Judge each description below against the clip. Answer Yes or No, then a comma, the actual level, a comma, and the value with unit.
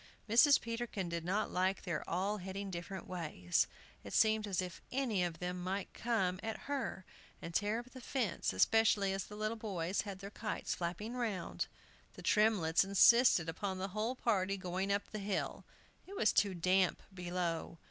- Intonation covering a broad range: No, average, 3.3 semitones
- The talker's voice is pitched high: Yes, high, 195 Hz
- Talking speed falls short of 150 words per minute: No, average, 175 wpm